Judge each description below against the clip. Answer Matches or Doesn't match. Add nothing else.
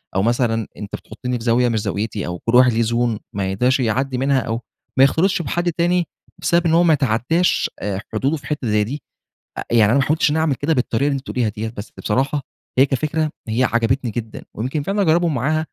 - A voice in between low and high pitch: Doesn't match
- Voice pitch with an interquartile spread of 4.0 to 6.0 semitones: Matches